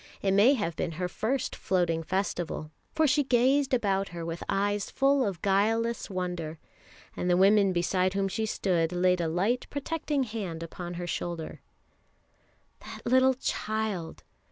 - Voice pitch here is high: Yes, high, 195 Hz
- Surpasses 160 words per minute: No, average, 155 wpm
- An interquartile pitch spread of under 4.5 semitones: No, average, 4.9 semitones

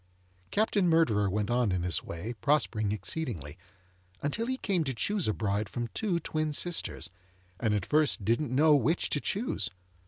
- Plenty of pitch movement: Yes, wide, 7.6 semitones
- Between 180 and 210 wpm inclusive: No, average, 165 wpm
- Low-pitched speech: Yes, low, 130 Hz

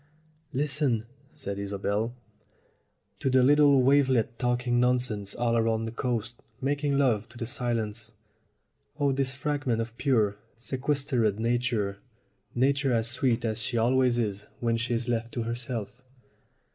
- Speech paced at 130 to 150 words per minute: Yes, average, 140 wpm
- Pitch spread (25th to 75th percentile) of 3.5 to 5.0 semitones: No, average, 2.7 semitones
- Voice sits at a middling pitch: No, low, 120 Hz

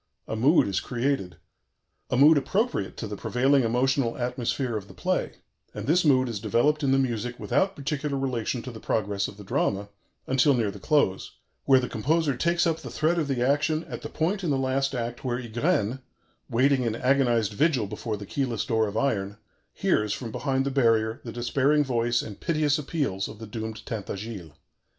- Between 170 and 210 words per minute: Yes, average, 190 wpm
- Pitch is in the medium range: No, low, 125 Hz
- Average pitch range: Yes, average, 4.1 semitones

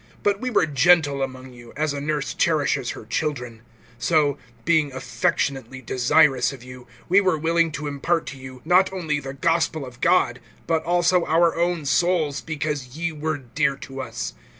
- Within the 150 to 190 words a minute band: Yes, average, 175 wpm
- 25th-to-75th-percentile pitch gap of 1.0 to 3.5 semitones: No, average, 3.9 semitones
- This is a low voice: No, medium, 150 Hz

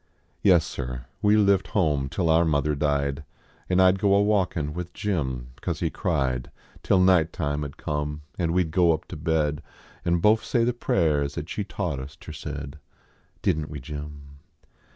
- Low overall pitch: Yes, very low, 80 Hz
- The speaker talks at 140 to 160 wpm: No, average, 190 wpm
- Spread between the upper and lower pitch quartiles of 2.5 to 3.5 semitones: No, average, 4.0 semitones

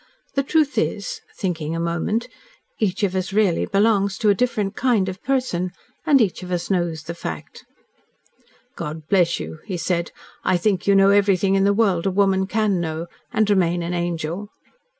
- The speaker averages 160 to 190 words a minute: Yes, average, 180 wpm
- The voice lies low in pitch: No, high, 190 Hz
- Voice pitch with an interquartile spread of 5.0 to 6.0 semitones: No, average, 3.3 semitones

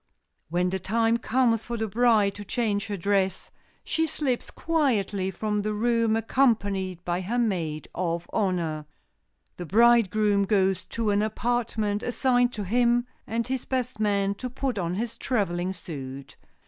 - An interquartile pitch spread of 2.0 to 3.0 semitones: No, average, 4.0 semitones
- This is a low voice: No, high, 210 Hz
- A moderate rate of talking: Yes, average, 150 wpm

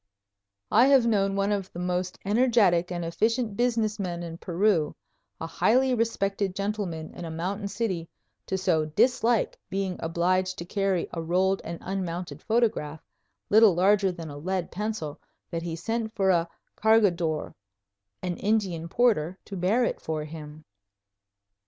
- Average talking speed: Yes, average, 150 wpm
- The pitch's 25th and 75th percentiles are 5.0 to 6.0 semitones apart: No, average, 4.1 semitones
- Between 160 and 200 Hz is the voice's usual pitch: Yes, high, 190 Hz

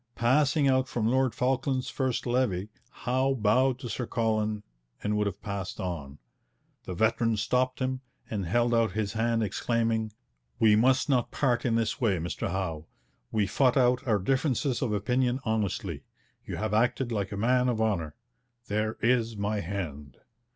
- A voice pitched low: Yes, low, 115 Hz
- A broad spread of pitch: No, average, 3.6 semitones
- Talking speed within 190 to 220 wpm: No, average, 165 wpm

